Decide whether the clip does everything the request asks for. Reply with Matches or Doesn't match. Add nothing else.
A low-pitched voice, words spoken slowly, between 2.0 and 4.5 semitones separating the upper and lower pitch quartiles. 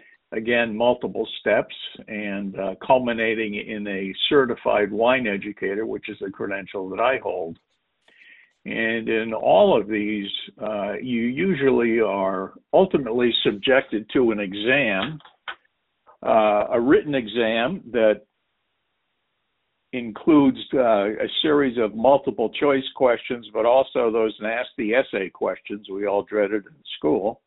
Matches